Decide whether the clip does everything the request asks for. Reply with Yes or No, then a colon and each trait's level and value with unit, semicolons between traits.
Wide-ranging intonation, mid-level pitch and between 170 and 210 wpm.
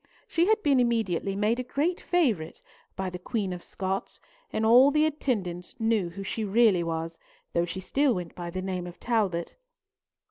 No: wide, 5.7 semitones; high, 200 Hz; average, 180 wpm